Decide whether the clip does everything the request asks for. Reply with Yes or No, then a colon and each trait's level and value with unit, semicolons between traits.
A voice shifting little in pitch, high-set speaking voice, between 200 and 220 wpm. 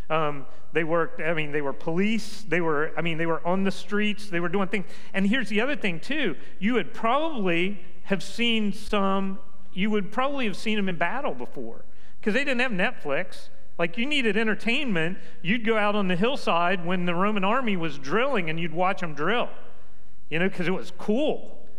No: average, 4.0 semitones; high, 195 Hz; fast, 205 wpm